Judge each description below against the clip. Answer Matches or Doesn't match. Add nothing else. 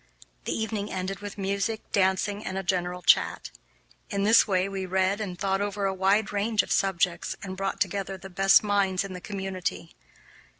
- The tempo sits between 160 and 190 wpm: Matches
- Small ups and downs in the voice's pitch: Matches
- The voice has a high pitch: Matches